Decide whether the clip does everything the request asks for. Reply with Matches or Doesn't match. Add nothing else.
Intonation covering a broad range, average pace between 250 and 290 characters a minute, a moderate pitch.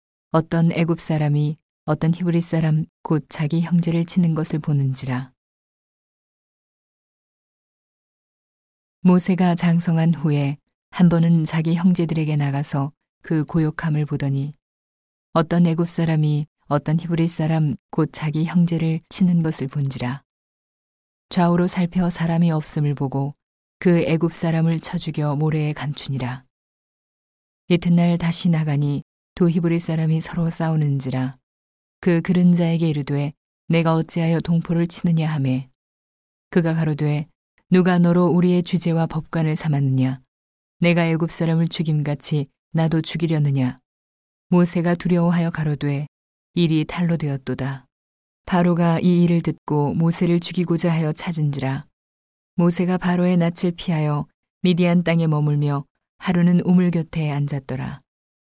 Doesn't match